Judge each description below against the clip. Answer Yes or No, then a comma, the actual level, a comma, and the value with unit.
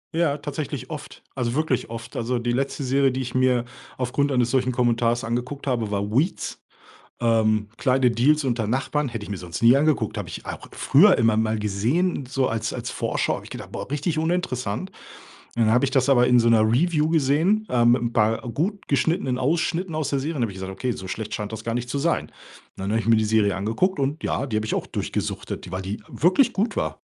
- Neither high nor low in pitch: No, low, 125 Hz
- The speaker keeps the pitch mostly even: No, average, 4.3 semitones